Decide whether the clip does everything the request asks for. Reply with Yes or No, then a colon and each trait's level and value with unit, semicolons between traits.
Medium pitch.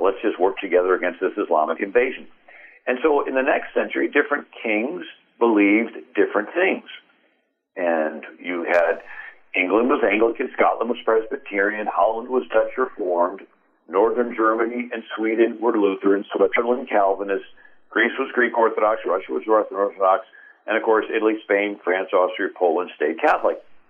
No: low, 110 Hz